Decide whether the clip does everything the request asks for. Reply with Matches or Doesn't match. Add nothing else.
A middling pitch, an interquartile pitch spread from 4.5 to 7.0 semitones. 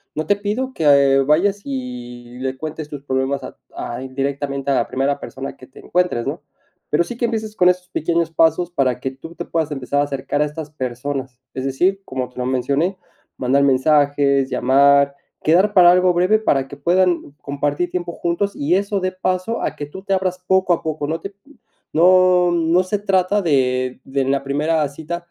Matches